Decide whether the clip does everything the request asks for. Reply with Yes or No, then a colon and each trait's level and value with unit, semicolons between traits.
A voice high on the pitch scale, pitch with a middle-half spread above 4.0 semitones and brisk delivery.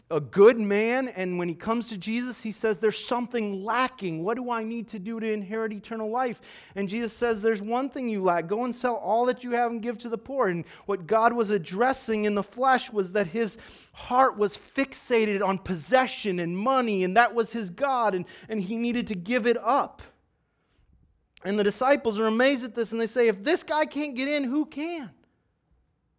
No: high, 225 Hz; average, 3.2 semitones; fast, 215 wpm